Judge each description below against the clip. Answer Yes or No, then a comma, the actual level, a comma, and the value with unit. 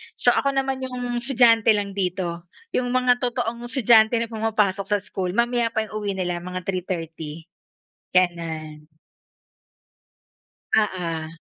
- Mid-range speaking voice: No, high, 205 Hz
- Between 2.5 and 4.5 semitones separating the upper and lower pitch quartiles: No, average, 5.1 semitones